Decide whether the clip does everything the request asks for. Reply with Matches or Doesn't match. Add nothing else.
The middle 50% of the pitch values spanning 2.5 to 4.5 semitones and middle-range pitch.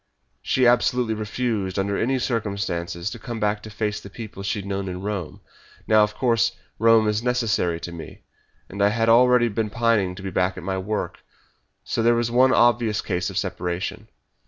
Doesn't match